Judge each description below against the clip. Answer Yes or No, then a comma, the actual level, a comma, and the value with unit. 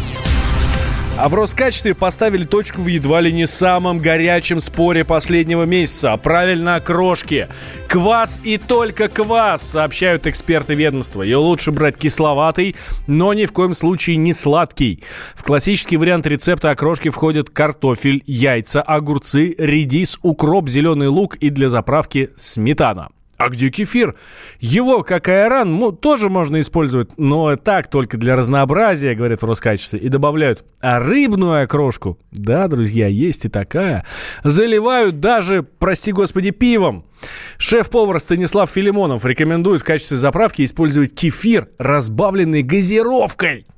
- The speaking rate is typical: Yes, average, 130 wpm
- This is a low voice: No, medium, 160 Hz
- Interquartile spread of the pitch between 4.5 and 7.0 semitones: Yes, average, 5.1 semitones